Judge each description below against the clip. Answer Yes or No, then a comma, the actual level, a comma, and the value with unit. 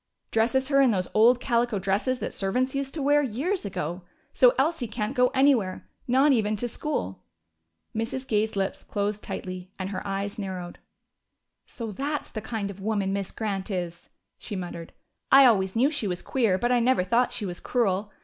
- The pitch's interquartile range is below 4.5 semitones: No, average, 4.9 semitones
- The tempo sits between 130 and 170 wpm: No, average, 185 wpm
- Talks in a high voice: Yes, high, 220 Hz